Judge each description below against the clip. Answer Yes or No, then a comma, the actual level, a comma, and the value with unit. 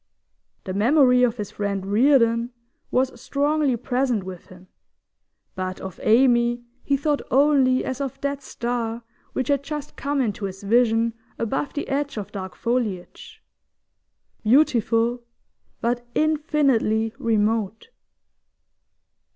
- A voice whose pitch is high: Yes, high, 240 Hz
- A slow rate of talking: Yes, slow, 120 wpm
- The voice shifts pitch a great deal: No, average, 4.2 semitones